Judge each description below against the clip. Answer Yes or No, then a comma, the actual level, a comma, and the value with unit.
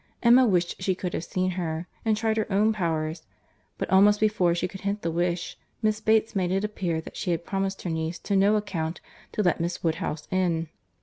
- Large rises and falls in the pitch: No, average, 3.5 semitones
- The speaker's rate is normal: No, fast, 210 wpm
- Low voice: No, medium, 185 Hz